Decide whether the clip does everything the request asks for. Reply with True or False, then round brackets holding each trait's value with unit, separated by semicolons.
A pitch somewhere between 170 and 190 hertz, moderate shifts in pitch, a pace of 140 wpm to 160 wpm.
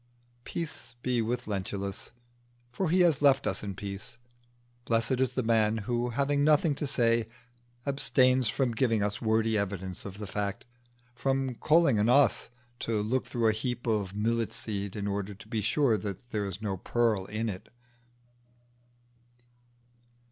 False (115 Hz; 3.7 semitones; 155 wpm)